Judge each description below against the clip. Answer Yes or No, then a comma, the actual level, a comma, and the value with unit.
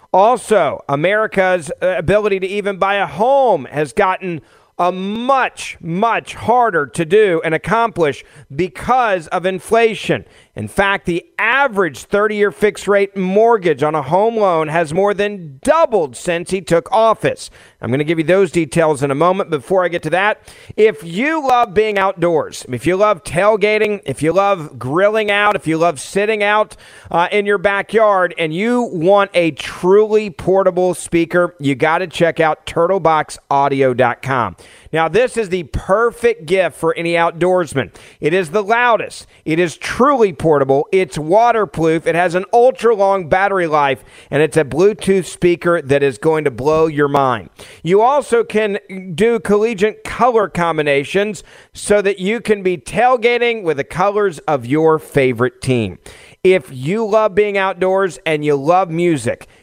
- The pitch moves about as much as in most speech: Yes, average, 4.7 semitones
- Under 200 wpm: Yes, average, 160 wpm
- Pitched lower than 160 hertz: No, medium, 185 Hz